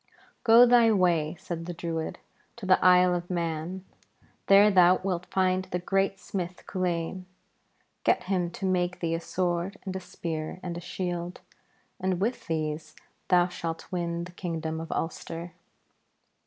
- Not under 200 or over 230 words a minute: No, average, 155 wpm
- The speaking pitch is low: No, medium, 180 Hz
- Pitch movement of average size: No, narrow, 1.9 semitones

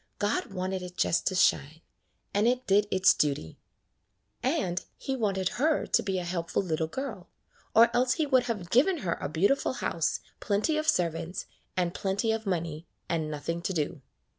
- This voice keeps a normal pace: Yes, average, 175 wpm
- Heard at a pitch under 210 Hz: Yes, high, 190 Hz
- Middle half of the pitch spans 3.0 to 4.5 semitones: No, wide, 5.5 semitones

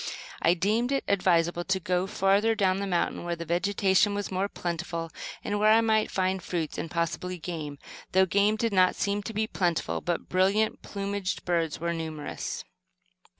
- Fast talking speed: No, average, 175 wpm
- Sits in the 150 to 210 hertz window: Yes, medium, 185 Hz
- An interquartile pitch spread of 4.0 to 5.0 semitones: No, average, 3.0 semitones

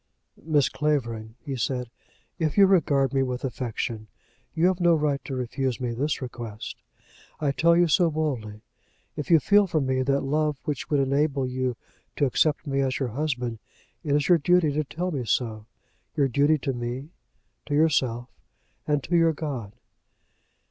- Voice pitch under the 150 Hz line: Yes, medium, 140 Hz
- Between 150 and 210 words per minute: Yes, average, 170 wpm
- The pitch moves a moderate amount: Yes, average, 3.6 semitones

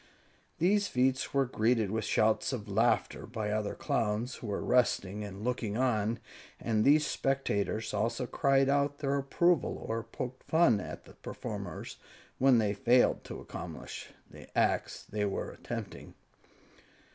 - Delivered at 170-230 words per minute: No, average, 145 wpm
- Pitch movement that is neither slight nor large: Yes, average, 4.2 semitones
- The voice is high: No, low, 120 Hz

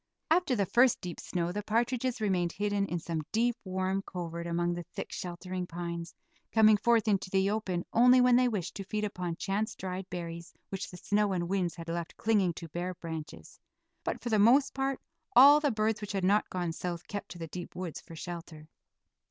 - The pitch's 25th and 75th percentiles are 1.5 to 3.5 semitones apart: No, average, 3.9 semitones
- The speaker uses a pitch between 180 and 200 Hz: Yes, high, 190 Hz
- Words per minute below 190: No, average, 200 wpm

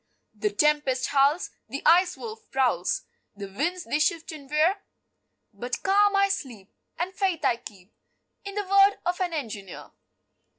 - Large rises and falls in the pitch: Yes, wide, 7.3 semitones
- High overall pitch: Yes, very high, 305 Hz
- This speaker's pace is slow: No, average, 155 wpm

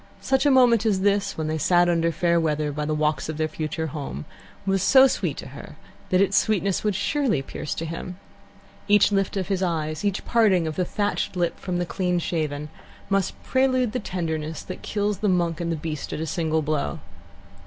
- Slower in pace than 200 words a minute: No, fast, 205 wpm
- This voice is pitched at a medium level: Yes, medium, 175 Hz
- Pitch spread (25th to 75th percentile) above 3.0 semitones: Yes, average, 4.4 semitones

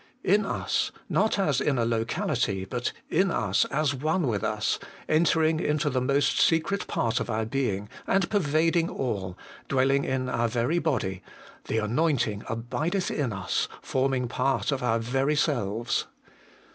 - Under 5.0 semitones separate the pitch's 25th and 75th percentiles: No, wide, 5.4 semitones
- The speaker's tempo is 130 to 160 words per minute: Yes, average, 150 wpm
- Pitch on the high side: No, low, 130 Hz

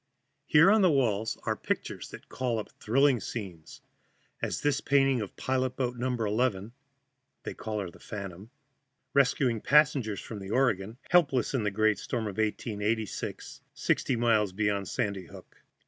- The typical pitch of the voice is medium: No, low, 115 Hz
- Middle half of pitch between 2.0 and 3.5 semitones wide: No, average, 4.0 semitones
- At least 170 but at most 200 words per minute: No, average, 155 wpm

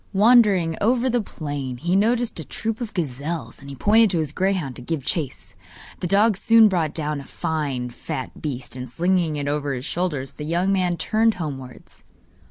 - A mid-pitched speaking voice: Yes, medium, 165 Hz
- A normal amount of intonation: No, wide, 6.0 semitones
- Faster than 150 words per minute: Yes, average, 180 wpm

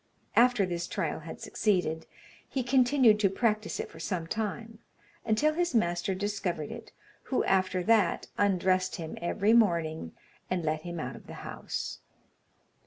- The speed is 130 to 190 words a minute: Yes, average, 150 wpm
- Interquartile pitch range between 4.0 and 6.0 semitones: Yes, average, 4.4 semitones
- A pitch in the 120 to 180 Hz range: No, high, 195 Hz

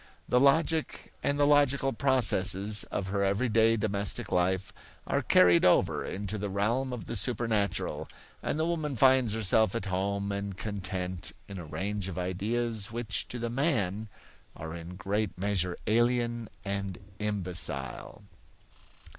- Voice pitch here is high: No, low, 105 Hz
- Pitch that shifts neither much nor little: Yes, average, 3.9 semitones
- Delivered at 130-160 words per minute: Yes, average, 140 wpm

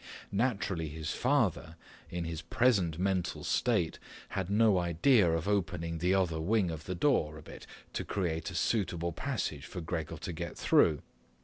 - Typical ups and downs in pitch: Yes, average, 3.6 semitones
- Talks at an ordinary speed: Yes, average, 165 wpm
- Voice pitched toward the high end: No, very low, 90 Hz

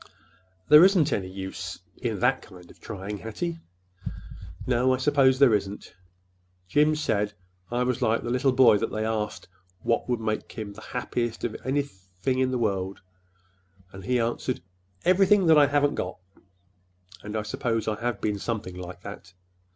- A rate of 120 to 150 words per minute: No, average, 160 wpm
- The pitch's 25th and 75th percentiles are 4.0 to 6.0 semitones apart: Yes, average, 4.5 semitones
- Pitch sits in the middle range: No, low, 115 Hz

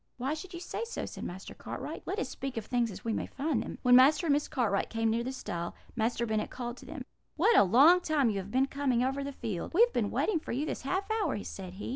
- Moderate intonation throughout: Yes, average, 4.9 semitones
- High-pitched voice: Yes, very high, 255 Hz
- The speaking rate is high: Yes, fast, 270 wpm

